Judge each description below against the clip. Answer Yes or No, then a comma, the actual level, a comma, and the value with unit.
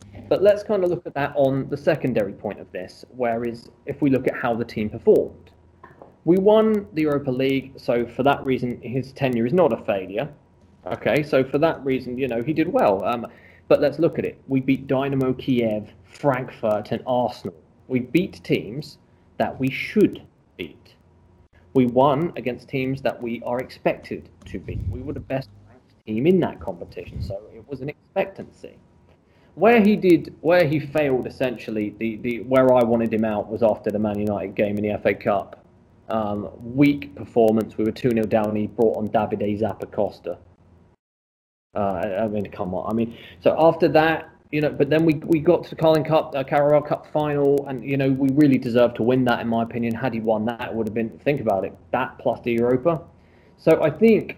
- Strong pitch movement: No, average, 4.6 semitones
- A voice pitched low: Yes, low, 125 Hz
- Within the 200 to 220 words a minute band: Yes, fast, 205 wpm